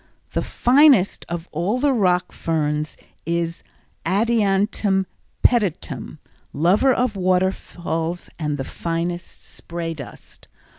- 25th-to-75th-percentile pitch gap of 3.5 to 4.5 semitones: Yes, average, 3.9 semitones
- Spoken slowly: Yes, slow, 100 wpm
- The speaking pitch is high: No, medium, 180 Hz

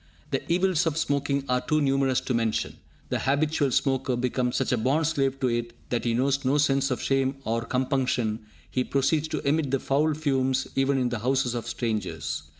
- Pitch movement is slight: Yes, narrow, 2.3 semitones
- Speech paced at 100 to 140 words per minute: No, average, 195 wpm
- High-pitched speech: No, low, 135 Hz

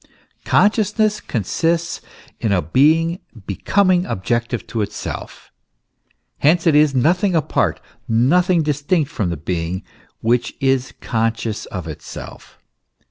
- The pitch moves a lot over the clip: Yes, wide, 7.3 semitones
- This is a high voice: No, medium, 140 Hz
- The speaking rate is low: Yes, slow, 110 wpm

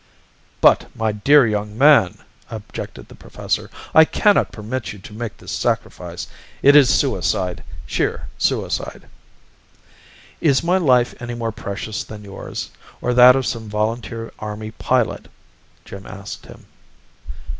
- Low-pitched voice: Yes, low, 115 Hz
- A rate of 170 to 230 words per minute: No, slow, 135 wpm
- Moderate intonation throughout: Yes, average, 3.4 semitones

